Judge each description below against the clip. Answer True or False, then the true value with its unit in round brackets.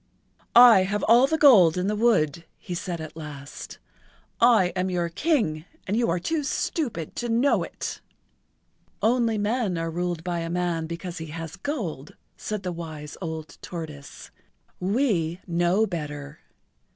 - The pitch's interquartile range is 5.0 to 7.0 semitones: True (5.3 semitones)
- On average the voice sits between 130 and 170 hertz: False (180 Hz)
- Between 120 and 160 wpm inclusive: True (155 wpm)